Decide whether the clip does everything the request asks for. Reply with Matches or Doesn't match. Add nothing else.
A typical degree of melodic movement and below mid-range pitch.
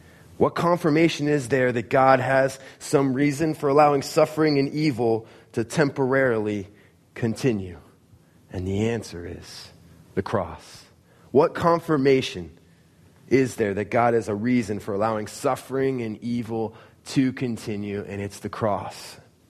Matches